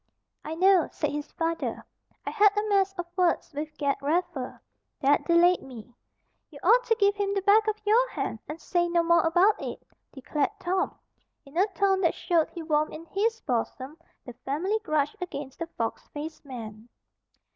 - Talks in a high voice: Yes, very high, 335 Hz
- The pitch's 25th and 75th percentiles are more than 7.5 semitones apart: No, average, 5.2 semitones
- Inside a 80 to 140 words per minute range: No, average, 180 wpm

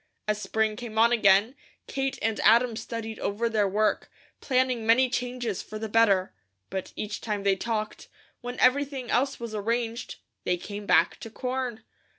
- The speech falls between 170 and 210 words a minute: No, average, 160 wpm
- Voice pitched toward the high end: Yes, high, 225 Hz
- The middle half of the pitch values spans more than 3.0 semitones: No, narrow, 2.6 semitones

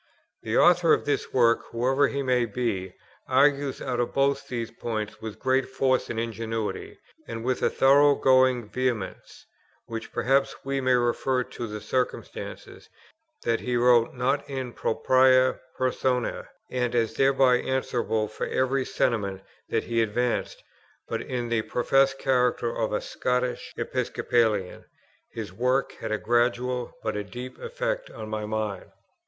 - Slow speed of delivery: No, average, 145 wpm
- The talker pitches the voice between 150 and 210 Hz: No, low, 125 Hz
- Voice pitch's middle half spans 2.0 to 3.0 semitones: Yes, narrow, 2.5 semitones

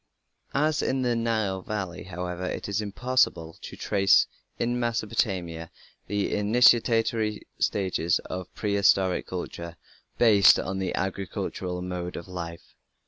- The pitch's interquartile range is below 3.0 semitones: No, average, 3.7 semitones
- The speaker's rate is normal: No, slow, 120 wpm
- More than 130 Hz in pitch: No, very low, 95 Hz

